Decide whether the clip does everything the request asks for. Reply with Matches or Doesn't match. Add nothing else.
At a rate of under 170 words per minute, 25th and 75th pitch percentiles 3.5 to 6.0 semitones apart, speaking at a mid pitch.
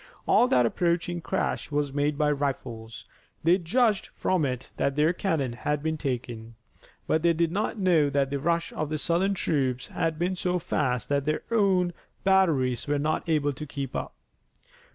Doesn't match